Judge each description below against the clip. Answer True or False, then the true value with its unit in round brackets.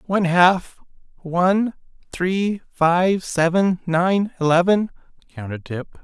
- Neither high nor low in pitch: True (180 Hz)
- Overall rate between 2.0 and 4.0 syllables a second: True (3.8 syllables/s)